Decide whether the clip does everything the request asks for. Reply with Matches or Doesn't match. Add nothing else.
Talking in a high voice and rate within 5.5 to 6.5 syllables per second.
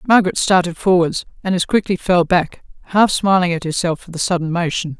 Doesn't match